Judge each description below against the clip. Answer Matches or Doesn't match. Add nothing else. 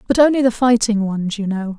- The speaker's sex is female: Matches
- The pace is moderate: Doesn't match